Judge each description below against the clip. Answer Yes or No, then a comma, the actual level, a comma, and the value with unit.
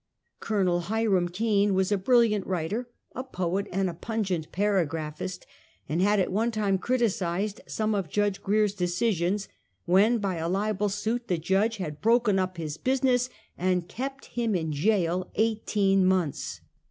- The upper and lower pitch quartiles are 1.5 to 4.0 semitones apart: Yes, average, 3.3 semitones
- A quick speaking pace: No, average, 155 wpm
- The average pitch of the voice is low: No, high, 195 Hz